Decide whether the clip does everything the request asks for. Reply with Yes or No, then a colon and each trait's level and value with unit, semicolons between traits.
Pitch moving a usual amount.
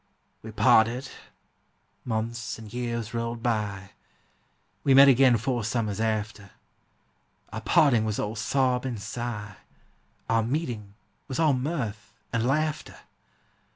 Yes: average, 3.0 semitones